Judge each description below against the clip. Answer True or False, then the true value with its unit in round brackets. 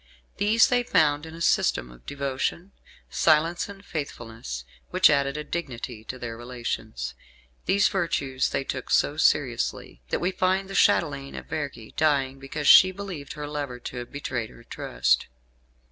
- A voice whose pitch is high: False (140 Hz)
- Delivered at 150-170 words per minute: True (160 wpm)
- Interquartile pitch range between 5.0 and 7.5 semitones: True (5.5 semitones)